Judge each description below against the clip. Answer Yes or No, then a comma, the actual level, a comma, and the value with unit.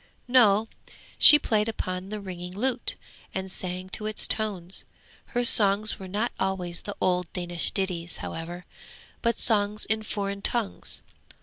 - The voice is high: Yes, high, 200 Hz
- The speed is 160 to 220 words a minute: No, average, 140 wpm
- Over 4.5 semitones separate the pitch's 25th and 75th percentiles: No, average, 3.0 semitones